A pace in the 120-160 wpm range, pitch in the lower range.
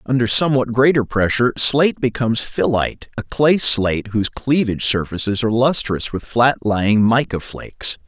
Yes: average, 150 wpm; low, 120 Hz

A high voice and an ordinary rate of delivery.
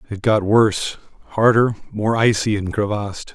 No: low, 105 Hz; average, 145 wpm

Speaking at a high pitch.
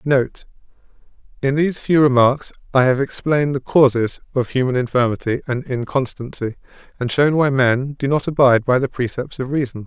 No: low, 130 Hz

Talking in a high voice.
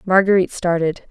No: medium, 180 Hz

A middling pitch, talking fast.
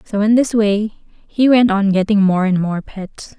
No: high, 205 Hz; fast, 215 wpm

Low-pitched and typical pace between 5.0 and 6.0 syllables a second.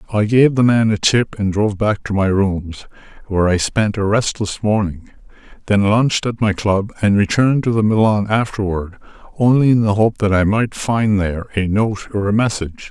Yes: low, 105 Hz; 5.2 syllables/s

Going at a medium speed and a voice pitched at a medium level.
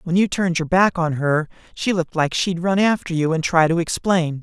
No: fast, 245 wpm; medium, 170 Hz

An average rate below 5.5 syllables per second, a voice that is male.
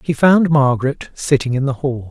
Yes: 5.1 syllables/s; male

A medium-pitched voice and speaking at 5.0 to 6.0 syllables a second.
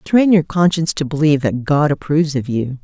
Yes: medium, 150 Hz; 5.9 syllables/s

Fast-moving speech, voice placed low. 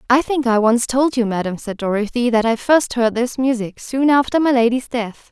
No: fast, 225 wpm; high, 240 Hz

